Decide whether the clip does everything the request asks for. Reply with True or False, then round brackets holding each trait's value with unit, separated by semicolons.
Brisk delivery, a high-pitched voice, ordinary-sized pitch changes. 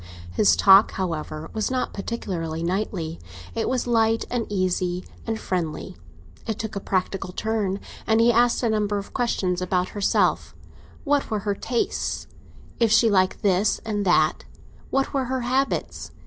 False (145 wpm; 205 Hz; 3.9 semitones)